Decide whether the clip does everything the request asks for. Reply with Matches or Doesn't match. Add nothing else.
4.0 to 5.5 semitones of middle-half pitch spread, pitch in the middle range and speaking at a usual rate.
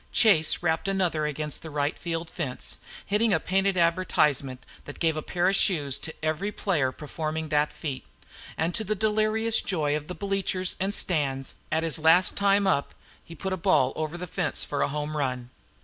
Matches